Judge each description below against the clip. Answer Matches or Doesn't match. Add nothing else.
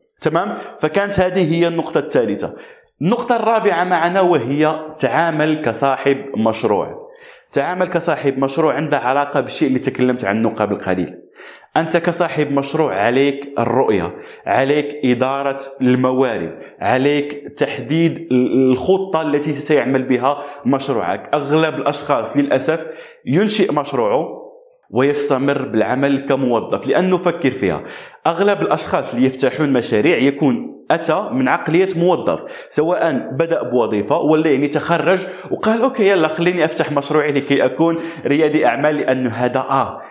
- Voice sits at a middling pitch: Matches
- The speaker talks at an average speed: Matches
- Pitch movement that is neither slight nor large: Matches